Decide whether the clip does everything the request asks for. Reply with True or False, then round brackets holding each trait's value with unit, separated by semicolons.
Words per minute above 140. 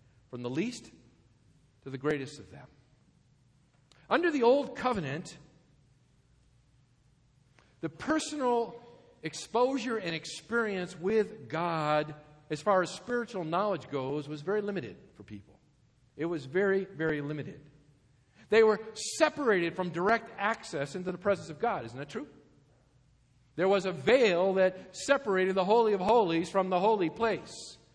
False (135 wpm)